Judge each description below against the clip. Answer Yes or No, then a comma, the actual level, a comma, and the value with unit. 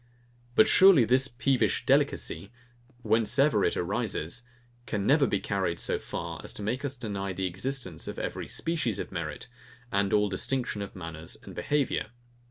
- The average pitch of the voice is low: Yes, low, 105 Hz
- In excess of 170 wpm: No, average, 165 wpm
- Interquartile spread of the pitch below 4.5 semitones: No, wide, 5.5 semitones